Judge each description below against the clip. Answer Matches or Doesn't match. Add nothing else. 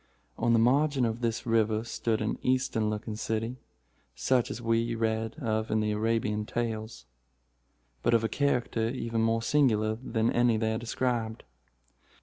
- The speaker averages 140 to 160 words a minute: Matches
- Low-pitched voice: Matches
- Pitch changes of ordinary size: Doesn't match